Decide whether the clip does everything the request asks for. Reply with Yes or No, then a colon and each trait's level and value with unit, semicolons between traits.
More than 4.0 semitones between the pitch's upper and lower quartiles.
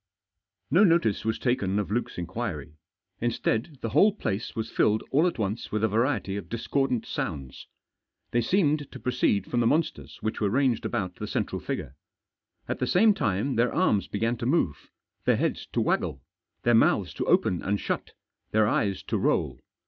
Yes: average, 4.8 semitones